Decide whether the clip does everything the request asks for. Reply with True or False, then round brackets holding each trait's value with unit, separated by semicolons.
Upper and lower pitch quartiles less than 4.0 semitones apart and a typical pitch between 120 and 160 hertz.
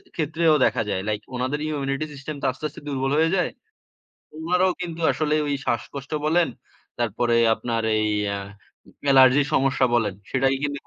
True (3.5 semitones; 140 Hz)